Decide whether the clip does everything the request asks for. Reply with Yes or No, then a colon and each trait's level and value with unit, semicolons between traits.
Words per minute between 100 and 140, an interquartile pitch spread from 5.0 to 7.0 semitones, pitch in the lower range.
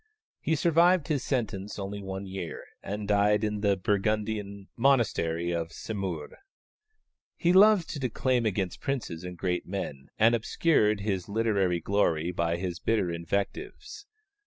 No: slow, 135 wpm; average, 4.3 semitones; low, 100 Hz